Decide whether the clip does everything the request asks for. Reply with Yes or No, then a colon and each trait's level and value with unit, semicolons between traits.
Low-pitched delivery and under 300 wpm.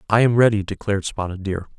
Yes: low, 105 Hz; average, 200 wpm